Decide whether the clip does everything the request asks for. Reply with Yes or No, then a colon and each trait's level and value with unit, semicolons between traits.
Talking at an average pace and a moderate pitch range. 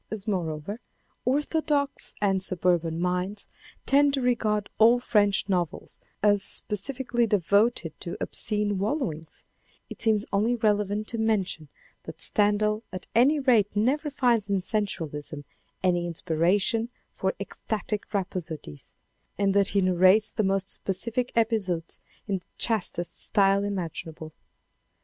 No: slow, 120 wpm; average, 3.6 semitones